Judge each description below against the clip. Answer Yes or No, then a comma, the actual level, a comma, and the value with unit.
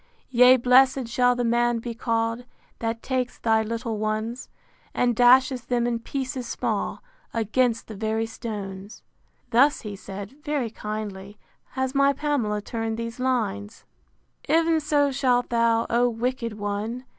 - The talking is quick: No, average, 145 wpm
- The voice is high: Yes, high, 235 Hz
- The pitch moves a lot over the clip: No, narrow, 2.5 semitones